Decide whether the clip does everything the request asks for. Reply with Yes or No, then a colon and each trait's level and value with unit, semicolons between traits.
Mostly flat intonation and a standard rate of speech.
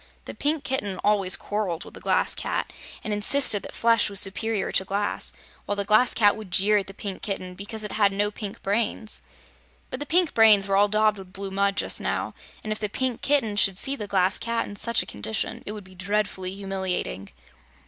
No: narrow, 1.9 semitones; fast, 215 wpm